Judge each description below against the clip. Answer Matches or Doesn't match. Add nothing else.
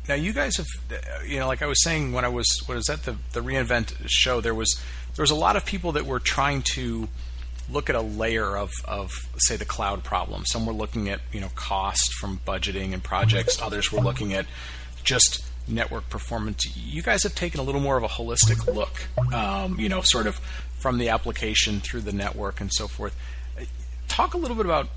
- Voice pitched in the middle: Doesn't match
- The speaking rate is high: Matches